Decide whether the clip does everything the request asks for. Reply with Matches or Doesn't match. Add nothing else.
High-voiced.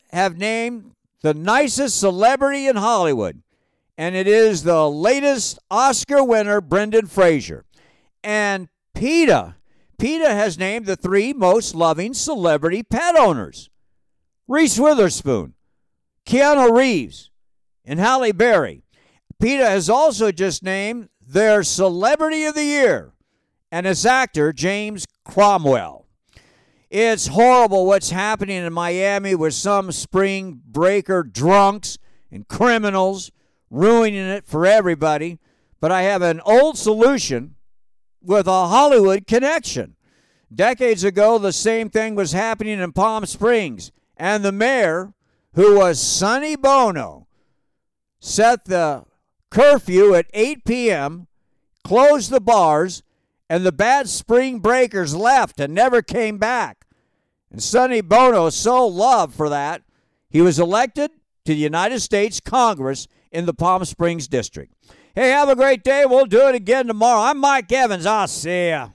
Matches